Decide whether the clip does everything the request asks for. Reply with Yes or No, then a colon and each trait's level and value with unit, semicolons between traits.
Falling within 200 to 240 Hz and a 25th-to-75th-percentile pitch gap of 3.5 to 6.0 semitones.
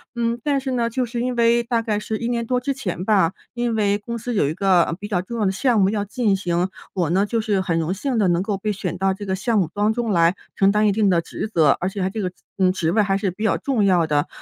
Yes: high, 205 Hz; average, 3.9 semitones